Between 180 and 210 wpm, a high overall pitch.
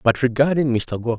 No: fast, 205 wpm; low, 125 Hz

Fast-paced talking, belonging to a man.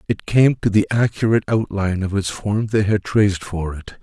Yes: fast, 225 wpm; male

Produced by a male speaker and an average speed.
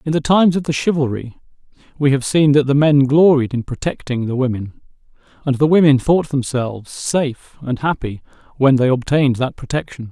Yes: male; average, 180 wpm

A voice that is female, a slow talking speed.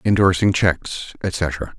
No: male; slow, 100 wpm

